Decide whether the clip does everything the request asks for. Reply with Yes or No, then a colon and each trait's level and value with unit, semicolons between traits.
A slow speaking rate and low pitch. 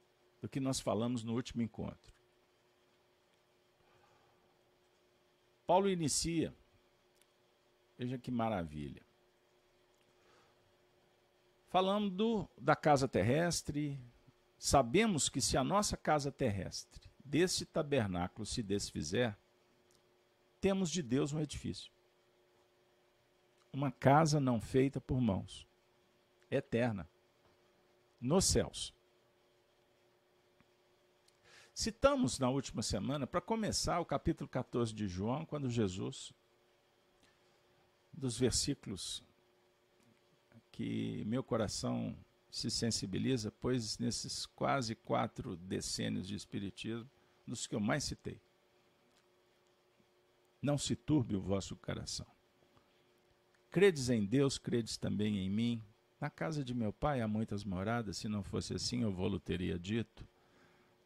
Yes: slow, 100 wpm; low, 120 Hz